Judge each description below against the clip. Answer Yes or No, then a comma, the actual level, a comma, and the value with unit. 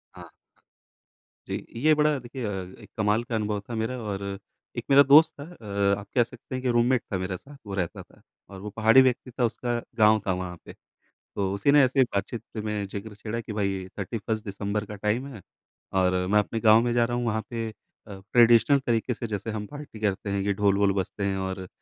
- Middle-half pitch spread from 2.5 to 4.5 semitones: Yes, average, 3.3 semitones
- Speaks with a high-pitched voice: No, low, 110 Hz